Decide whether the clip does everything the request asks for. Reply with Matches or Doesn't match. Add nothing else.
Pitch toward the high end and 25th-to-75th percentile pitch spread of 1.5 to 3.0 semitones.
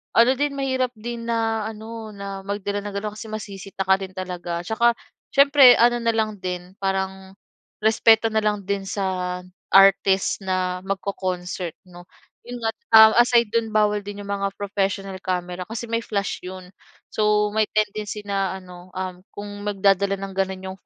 Matches